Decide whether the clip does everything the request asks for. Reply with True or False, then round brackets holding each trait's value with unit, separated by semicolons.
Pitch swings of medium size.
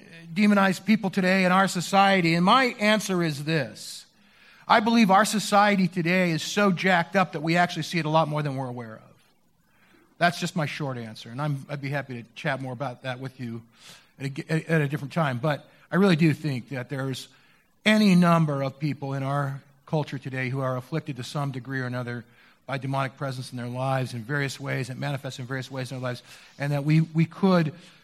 True (4.8 semitones)